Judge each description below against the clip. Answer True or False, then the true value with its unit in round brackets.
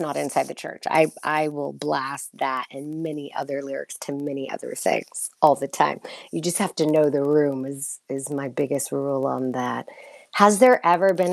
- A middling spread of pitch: False (2.3 semitones)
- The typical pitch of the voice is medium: True (145 Hz)